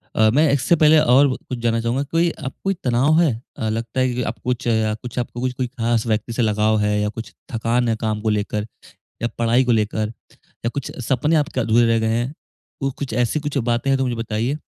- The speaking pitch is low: Yes, low, 120 Hz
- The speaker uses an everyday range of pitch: Yes, average, 3.0 semitones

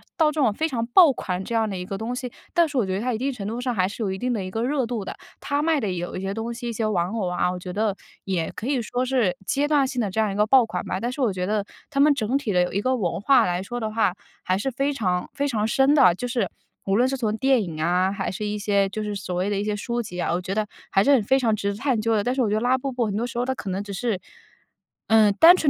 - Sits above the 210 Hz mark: Yes, high, 220 Hz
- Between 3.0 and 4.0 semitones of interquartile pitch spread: No, average, 4.6 semitones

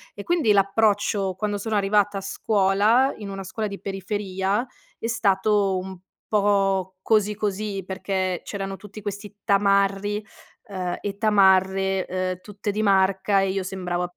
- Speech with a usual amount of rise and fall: No, narrow, 1.5 semitones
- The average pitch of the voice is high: Yes, high, 195 Hz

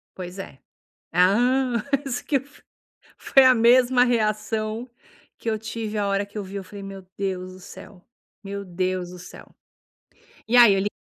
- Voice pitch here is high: Yes, high, 210 Hz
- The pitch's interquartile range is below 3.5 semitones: No, average, 4.0 semitones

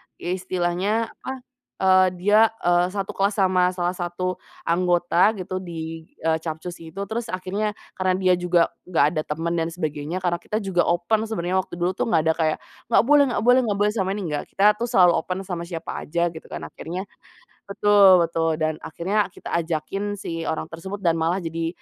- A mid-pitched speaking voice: Yes, medium, 180 Hz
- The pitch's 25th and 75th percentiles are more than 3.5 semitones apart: No, average, 2.8 semitones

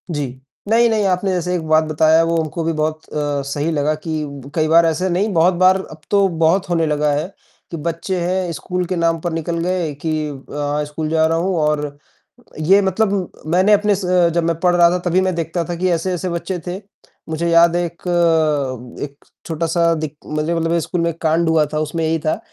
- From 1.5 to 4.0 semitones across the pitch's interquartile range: Yes, narrow, 2.4 semitones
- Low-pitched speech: No, medium, 165 Hz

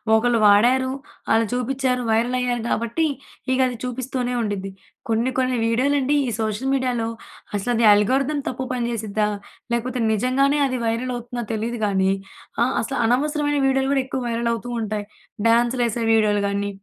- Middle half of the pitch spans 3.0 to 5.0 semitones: No, narrow, 2.5 semitones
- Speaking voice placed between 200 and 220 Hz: No, high, 240 Hz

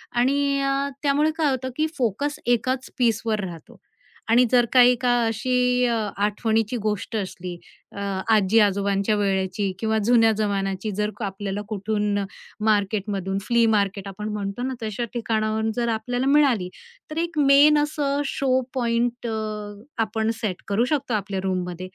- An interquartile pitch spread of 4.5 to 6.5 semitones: No, average, 3.7 semitones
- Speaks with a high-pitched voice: Yes, high, 220 Hz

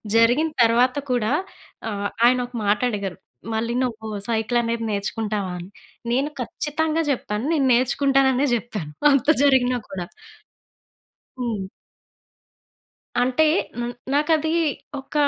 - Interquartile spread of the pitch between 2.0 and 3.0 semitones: No, average, 3.8 semitones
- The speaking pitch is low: No, high, 240 Hz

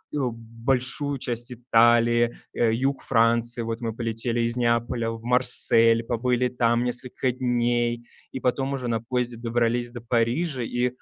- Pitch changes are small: Yes, narrow, 1.3 semitones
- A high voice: No, low, 120 Hz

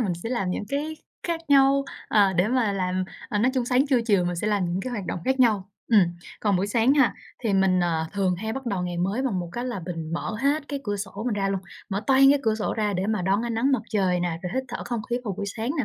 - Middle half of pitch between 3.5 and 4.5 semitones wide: No, average, 4.9 semitones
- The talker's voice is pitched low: No, high, 210 Hz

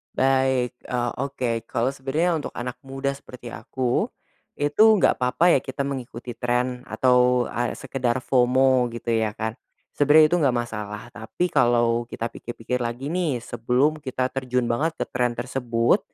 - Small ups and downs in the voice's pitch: Yes, narrow, 2.1 semitones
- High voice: No, low, 125 Hz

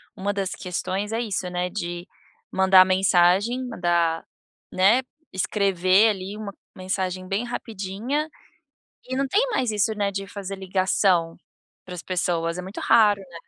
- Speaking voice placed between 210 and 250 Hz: No, high, 190 Hz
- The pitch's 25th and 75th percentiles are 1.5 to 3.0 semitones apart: Yes, narrow, 2.4 semitones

